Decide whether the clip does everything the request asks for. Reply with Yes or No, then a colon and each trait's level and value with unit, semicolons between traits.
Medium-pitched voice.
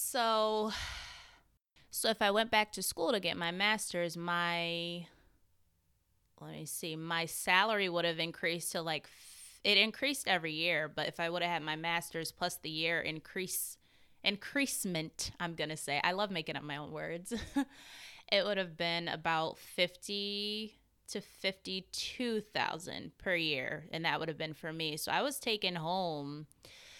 Yes: medium, 175 Hz